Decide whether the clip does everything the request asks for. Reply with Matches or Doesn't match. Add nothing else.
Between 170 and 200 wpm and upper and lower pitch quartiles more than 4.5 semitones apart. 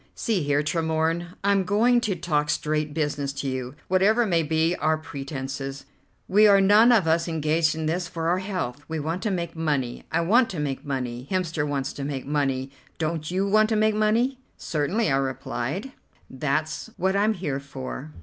Matches